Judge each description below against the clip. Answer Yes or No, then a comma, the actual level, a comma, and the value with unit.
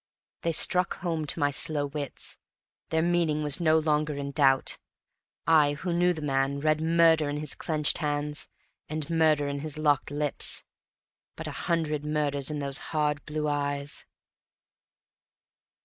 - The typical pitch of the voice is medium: Yes, medium, 150 Hz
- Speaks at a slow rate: No, average, 150 wpm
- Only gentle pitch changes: Yes, narrow, 1.7 semitones